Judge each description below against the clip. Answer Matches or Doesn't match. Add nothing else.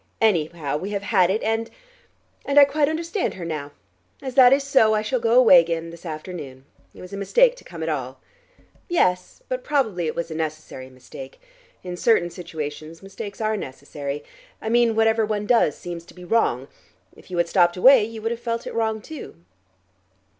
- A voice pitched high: Matches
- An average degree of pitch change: Doesn't match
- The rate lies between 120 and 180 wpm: Doesn't match